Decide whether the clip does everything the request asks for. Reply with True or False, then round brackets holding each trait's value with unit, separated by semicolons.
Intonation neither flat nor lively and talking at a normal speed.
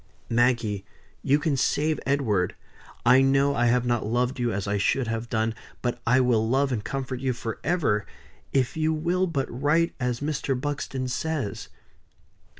True (3.3 semitones; 160 wpm)